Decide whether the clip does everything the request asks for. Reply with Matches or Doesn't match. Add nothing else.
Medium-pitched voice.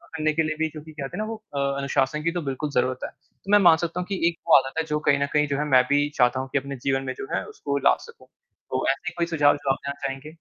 Matches